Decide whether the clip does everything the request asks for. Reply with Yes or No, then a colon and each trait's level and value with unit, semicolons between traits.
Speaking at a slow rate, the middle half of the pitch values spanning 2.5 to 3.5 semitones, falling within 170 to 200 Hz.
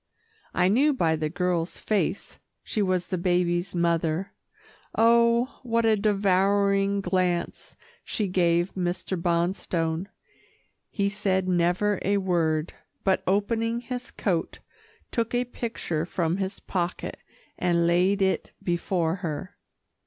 Yes: slow, 120 wpm; average, 2.8 semitones; medium, 185 Hz